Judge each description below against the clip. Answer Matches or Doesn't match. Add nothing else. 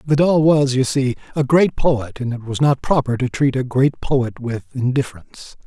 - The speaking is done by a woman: Doesn't match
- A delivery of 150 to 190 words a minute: Doesn't match